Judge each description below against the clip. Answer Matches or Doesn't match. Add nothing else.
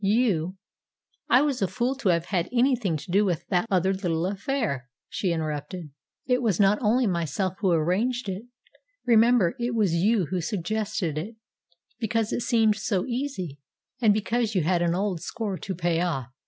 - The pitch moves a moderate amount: Matches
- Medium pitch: Doesn't match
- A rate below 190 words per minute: Matches